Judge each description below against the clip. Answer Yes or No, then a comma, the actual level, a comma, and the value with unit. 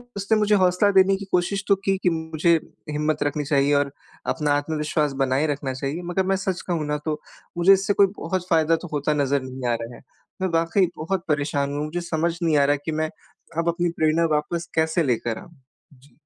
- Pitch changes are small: No, average, 3.5 semitones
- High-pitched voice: No, medium, 160 Hz